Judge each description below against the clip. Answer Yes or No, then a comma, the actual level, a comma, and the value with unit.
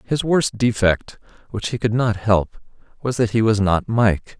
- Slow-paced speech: No, average, 165 wpm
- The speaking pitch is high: No, low, 110 Hz